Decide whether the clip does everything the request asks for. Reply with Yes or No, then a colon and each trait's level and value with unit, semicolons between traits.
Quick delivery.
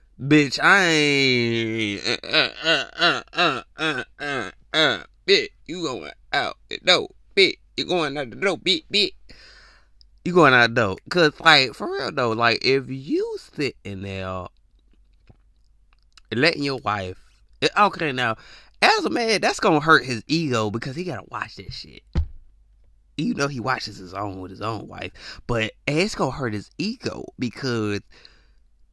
No: average, 165 wpm